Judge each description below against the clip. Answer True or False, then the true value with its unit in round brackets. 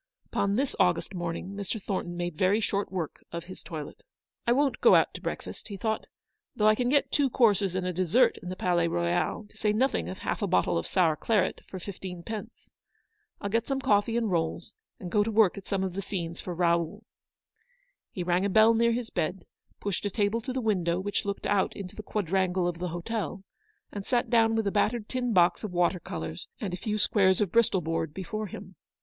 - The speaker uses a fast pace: True (225 wpm)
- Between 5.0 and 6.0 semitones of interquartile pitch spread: False (3.9 semitones)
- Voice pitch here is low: False (195 Hz)